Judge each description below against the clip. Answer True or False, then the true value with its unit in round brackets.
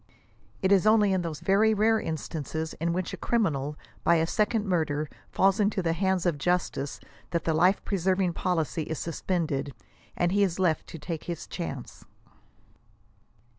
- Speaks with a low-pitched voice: False (175 Hz)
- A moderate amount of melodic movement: True (3.4 semitones)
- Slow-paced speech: False (170 wpm)